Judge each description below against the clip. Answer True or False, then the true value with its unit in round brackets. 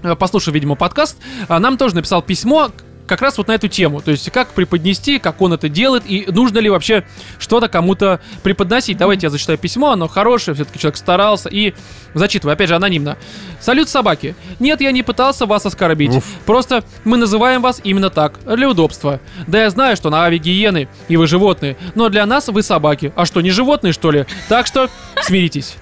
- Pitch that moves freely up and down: True (6.0 semitones)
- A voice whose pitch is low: False (195 Hz)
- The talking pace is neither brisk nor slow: False (190 wpm)